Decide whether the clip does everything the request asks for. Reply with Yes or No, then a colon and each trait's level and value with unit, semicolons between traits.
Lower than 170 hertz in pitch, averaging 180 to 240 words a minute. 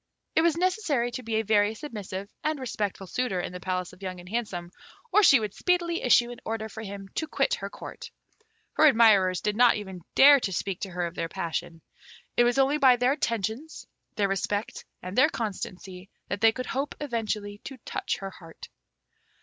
No: high, 220 Hz; average, 200 wpm